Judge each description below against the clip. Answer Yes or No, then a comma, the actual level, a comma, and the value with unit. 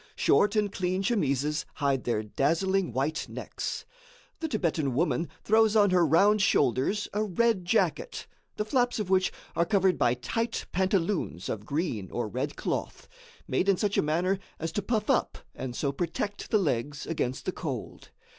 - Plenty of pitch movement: Yes, wide, 6.6 semitones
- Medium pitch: Yes, medium, 180 Hz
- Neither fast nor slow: Yes, average, 165 wpm